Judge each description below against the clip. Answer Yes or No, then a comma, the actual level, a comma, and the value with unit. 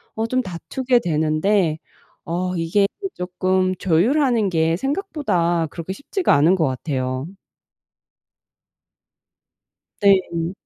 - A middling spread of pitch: Yes, average, 4.7 semitones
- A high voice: No, medium, 180 Hz